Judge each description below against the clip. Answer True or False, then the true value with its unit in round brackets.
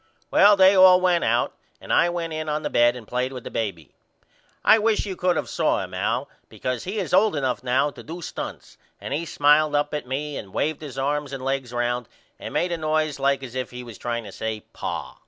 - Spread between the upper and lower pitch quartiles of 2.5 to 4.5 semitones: False (5.2 semitones)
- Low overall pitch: False (145 Hz)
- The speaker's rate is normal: False (235 wpm)